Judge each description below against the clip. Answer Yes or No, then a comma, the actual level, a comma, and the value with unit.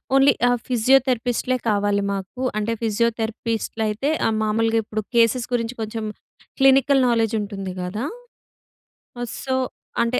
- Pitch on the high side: Yes, high, 230 Hz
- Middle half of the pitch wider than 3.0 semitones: No, average, 2.7 semitones